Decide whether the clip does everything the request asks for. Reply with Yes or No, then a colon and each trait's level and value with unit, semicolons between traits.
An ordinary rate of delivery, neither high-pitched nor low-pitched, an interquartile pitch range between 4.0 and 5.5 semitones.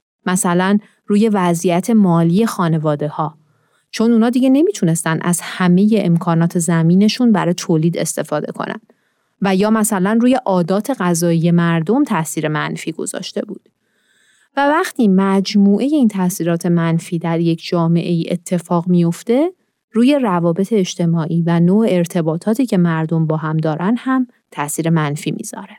Yes: average, 130 wpm; medium, 180 Hz; average, 4.4 semitones